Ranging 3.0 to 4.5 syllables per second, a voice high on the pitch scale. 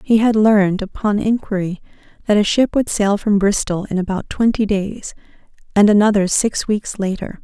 No: 5.0 syllables/s; high, 205 Hz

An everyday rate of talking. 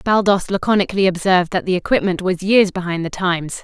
Yes: average, 180 wpm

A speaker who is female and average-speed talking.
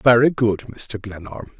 No: male; average, 150 wpm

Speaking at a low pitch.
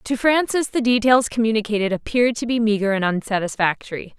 No: high, 225 Hz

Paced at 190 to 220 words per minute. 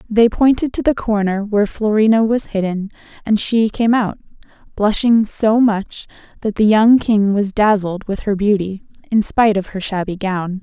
No: average, 175 wpm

